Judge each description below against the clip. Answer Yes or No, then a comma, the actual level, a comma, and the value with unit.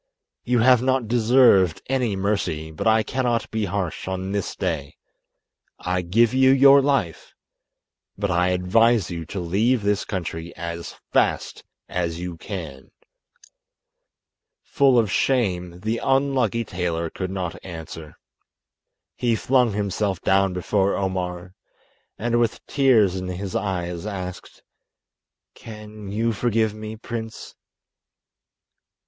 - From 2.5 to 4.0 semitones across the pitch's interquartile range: No, average, 4.5 semitones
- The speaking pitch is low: Yes, low, 100 Hz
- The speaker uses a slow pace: Yes, slow, 120 wpm